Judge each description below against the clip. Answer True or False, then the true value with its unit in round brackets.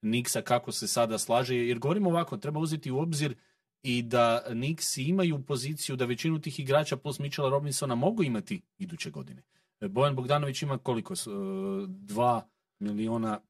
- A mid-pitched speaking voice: True (145 Hz)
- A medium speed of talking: True (150 wpm)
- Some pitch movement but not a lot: False (6.0 semitones)